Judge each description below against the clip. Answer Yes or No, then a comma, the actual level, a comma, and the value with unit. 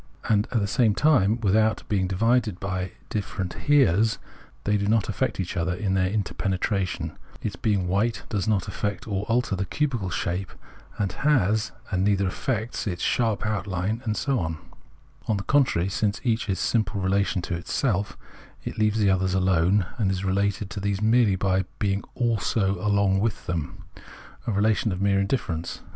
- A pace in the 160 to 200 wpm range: Yes, average, 175 wpm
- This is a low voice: Yes, low, 100 Hz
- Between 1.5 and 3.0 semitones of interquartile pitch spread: Yes, average, 2.7 semitones